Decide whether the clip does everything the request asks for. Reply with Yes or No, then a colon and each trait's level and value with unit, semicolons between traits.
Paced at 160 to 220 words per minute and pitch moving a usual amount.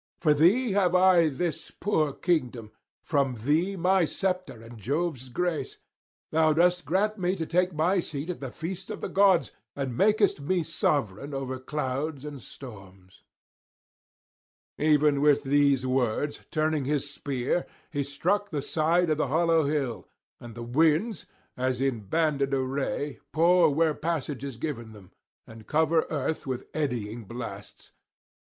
No: average, 150 wpm; average, 4.4 semitones